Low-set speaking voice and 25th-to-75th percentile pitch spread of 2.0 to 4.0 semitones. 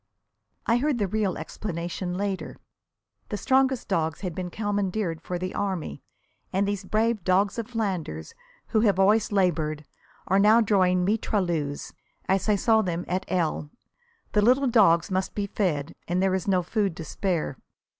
No: high, 190 Hz; average, 3.2 semitones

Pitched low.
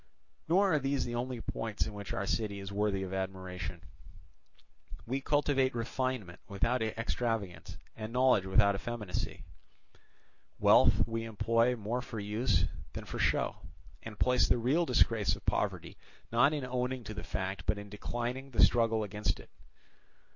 Yes: low, 115 Hz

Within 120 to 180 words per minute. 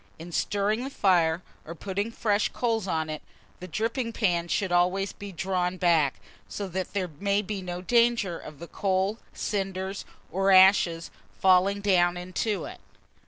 Yes: average, 165 wpm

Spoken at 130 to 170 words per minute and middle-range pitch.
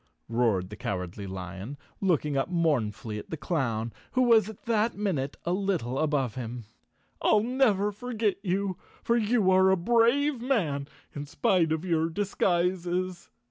Yes: average, 150 wpm; medium, 175 Hz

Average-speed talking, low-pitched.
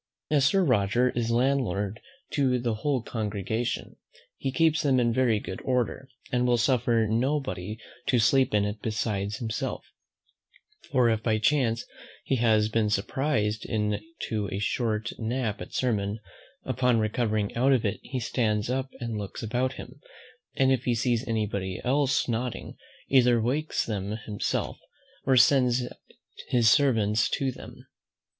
Yes: average, 150 wpm; low, 120 Hz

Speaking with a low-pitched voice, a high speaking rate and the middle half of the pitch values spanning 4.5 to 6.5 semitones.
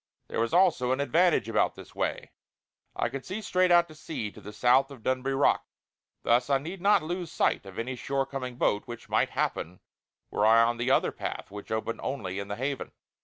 Yes: low, 130 Hz; fast, 215 wpm; average, 5.2 semitones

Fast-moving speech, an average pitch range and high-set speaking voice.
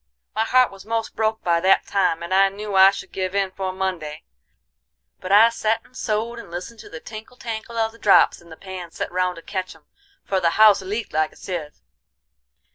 Yes: fast, 215 wpm; average, 3.3 semitones; high, 195 Hz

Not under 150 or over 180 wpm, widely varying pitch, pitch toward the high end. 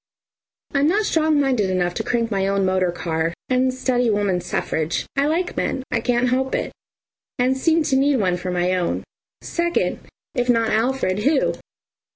Yes: average, 170 wpm; wide, 6.5 semitones; high, 245 Hz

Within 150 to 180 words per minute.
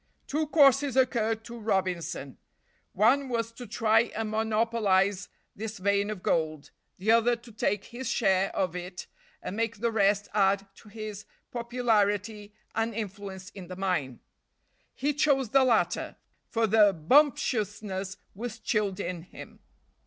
No: average, 140 wpm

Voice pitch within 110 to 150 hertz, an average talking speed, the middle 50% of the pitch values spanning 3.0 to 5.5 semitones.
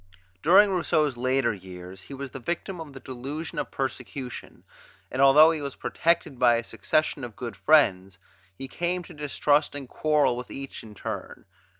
Yes: low, 135 Hz; average, 175 wpm; average, 4.1 semitones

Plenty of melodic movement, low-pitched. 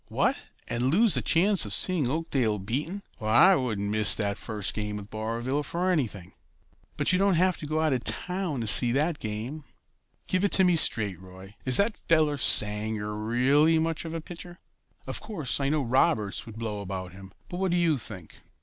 Yes: wide, 7.7 semitones; low, 130 Hz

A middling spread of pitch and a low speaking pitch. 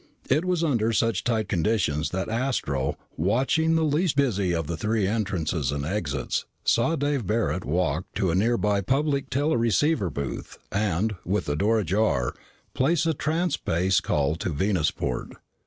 No: wide, 7.9 semitones; low, 105 Hz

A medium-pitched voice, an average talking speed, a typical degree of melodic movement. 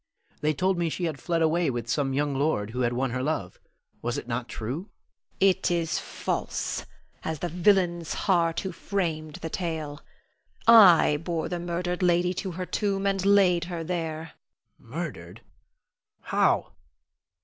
Yes: medium, 165 Hz; average, 160 wpm; average, 3.5 semitones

